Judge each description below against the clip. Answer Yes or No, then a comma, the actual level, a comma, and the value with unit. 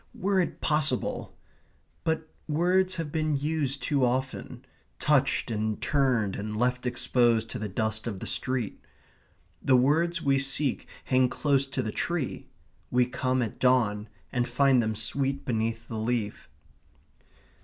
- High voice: No, low, 130 Hz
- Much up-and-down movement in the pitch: No, average, 4.1 semitones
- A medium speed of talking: Yes, average, 145 wpm